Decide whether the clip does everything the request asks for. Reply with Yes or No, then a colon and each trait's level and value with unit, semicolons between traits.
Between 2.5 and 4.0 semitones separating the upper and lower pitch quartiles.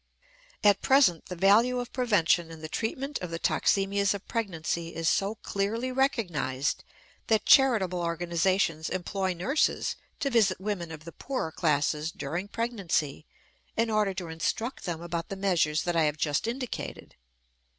No: average, 5.2 semitones